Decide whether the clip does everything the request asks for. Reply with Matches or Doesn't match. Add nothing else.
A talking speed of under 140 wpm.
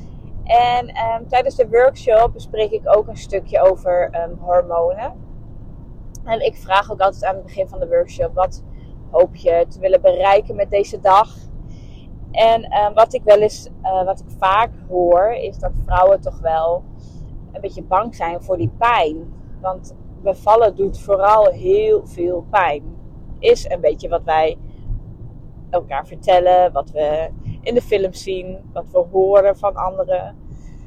Doesn't match